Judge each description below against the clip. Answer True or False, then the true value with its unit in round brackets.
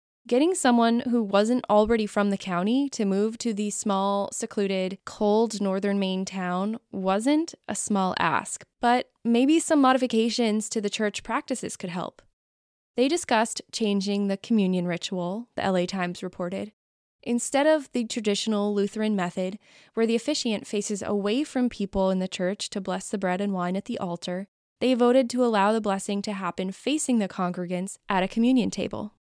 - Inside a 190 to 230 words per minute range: False (170 wpm)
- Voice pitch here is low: False (210 Hz)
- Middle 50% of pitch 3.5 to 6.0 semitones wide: True (3.9 semitones)